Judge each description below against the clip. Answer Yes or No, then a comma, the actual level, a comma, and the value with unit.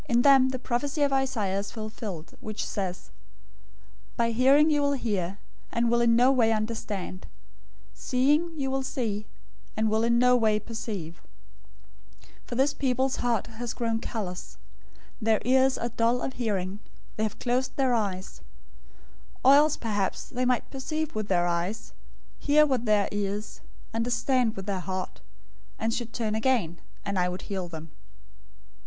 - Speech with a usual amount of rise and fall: Yes, average, 4.1 semitones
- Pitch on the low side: No, high, 230 Hz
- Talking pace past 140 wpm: Yes, average, 160 wpm